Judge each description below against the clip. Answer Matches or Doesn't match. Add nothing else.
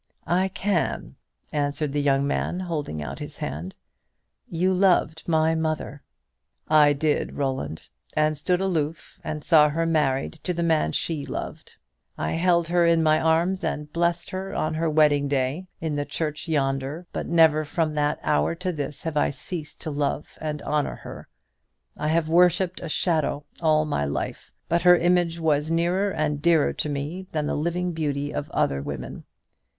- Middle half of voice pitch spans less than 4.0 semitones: Matches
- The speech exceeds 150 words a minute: Matches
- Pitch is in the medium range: Matches